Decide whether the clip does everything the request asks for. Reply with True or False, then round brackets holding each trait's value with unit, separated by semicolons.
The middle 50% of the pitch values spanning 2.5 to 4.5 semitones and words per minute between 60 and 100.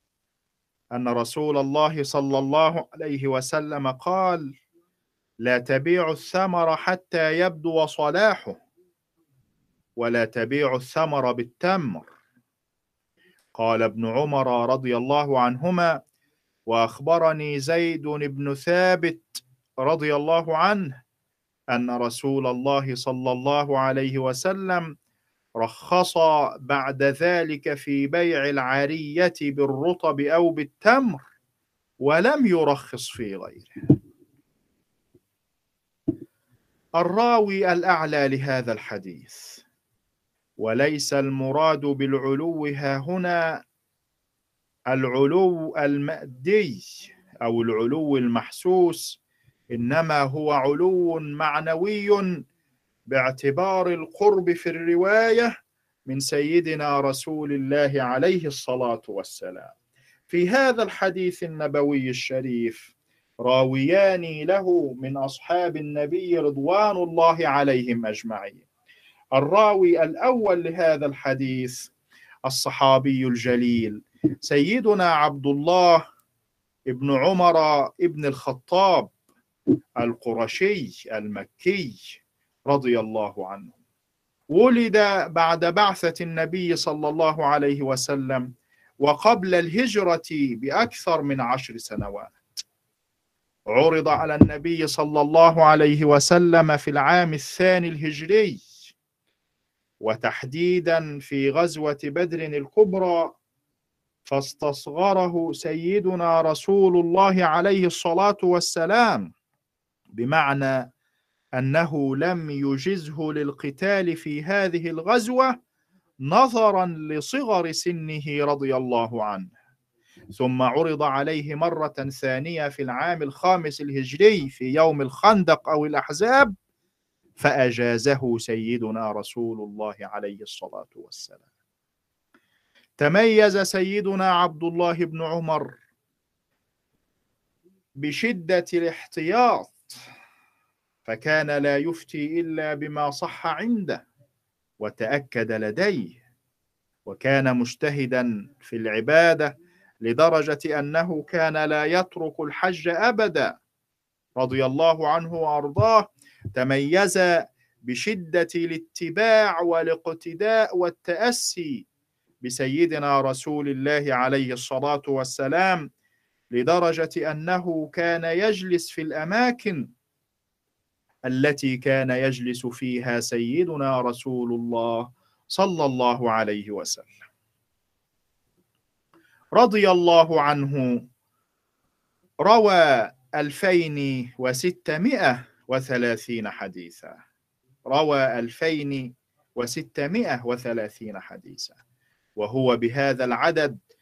False (4.9 semitones; 80 wpm)